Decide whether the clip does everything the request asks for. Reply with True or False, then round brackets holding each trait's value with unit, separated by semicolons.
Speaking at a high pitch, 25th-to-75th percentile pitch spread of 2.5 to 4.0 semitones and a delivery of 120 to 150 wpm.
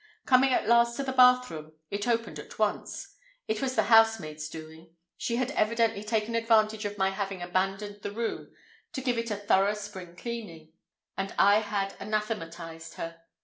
False (210 Hz; 3.7 semitones; 165 wpm)